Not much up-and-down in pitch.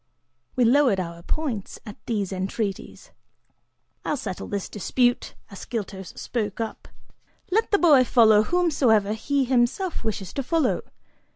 No: wide, 5.4 semitones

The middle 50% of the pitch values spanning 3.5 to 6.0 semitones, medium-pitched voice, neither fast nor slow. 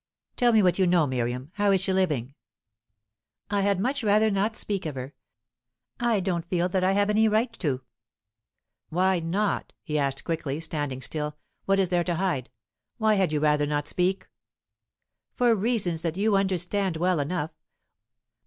Yes: average, 4.8 semitones; medium, 180 Hz; average, 170 wpm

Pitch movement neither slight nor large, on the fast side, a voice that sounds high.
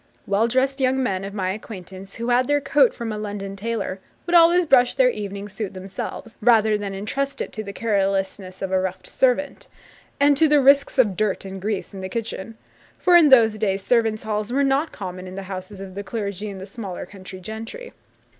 Yes: average, 4.5 semitones; fast, 210 wpm; high, 215 Hz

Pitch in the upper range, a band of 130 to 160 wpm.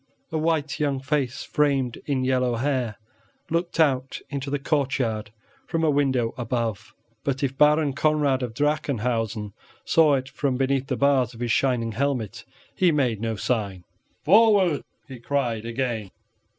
No: low, 135 Hz; average, 150 wpm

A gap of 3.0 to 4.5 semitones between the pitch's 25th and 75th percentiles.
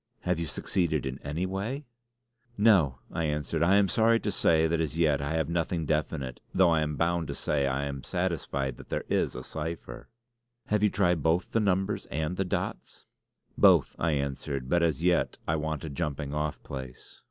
Yes: average, 3.8 semitones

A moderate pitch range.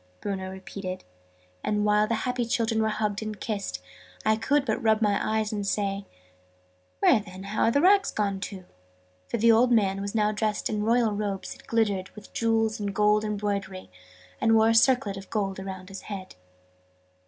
No: narrow, 2.1 semitones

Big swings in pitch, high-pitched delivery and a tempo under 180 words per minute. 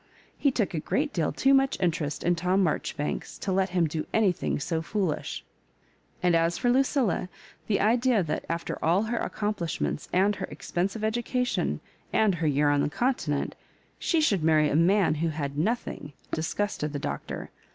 No: wide, 5.7 semitones; medium, 180 Hz; average, 170 wpm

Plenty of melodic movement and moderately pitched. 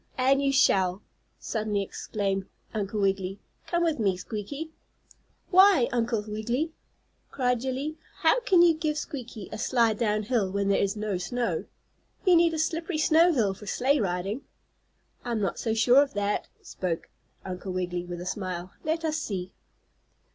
No: wide, 6.6 semitones; high, 225 Hz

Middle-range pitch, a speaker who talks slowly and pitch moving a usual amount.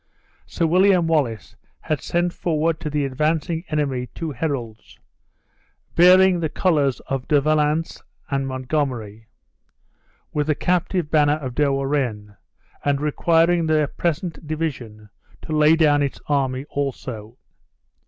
Yes: medium, 150 Hz; slow, 125 wpm; average, 3.3 semitones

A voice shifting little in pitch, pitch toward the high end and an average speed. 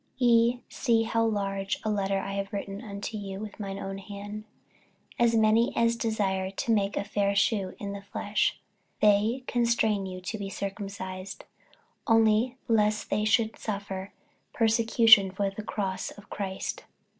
Yes: narrow, 2.2 semitones; high, 205 Hz; average, 160 wpm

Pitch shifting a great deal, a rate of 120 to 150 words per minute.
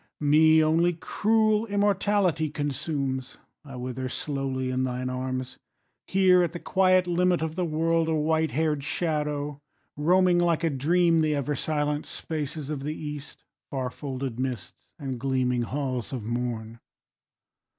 No: average, 4.2 semitones; average, 140 wpm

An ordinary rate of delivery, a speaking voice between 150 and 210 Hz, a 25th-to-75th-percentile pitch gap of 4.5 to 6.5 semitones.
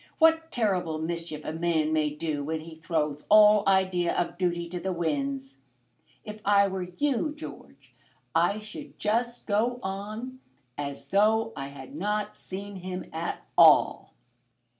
Yes: average, 145 wpm; medium, 185 Hz; average, 5.0 semitones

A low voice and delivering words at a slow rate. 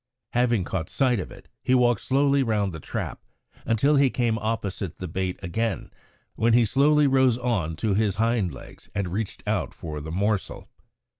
No: low, 110 Hz; average, 175 wpm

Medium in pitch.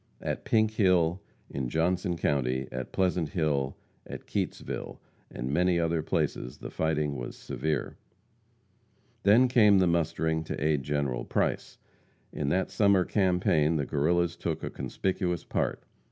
No: very low, 80 Hz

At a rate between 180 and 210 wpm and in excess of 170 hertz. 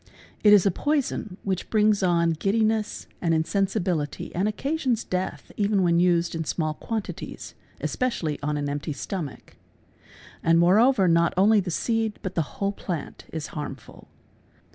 No: average, 155 wpm; medium, 185 Hz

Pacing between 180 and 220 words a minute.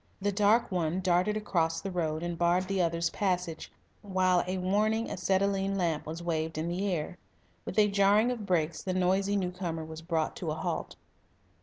Yes: average, 185 wpm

